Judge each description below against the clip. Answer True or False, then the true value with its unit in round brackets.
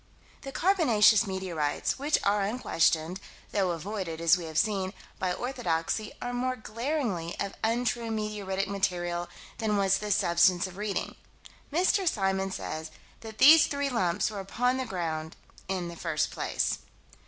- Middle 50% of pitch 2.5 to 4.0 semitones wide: False (5.0 semitones)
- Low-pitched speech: False (195 Hz)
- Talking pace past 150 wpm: False (145 wpm)